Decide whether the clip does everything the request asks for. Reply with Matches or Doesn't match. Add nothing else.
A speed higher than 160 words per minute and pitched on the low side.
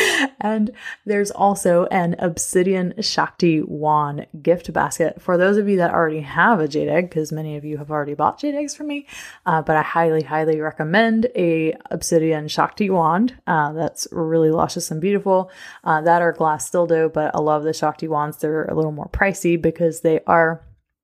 Doesn't match